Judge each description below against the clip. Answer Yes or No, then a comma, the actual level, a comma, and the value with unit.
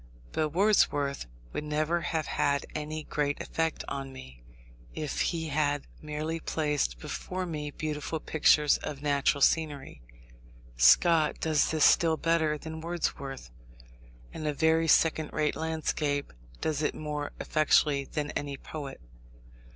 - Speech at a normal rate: No, slow, 130 wpm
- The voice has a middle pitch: Yes, medium, 150 Hz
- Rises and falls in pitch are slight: Yes, narrow, 1.9 semitones